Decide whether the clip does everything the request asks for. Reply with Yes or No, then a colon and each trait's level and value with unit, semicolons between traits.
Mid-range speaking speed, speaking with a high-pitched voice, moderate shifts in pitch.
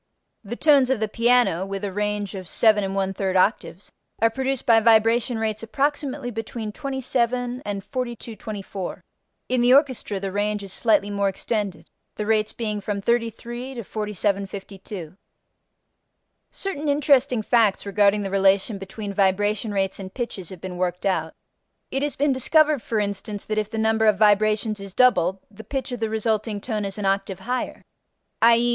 Yes: average, 165 wpm; high, 215 Hz; average, 3.3 semitones